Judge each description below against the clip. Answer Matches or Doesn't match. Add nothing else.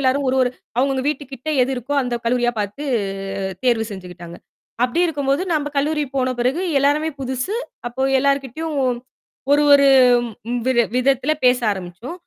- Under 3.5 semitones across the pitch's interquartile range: Matches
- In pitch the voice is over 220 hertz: Matches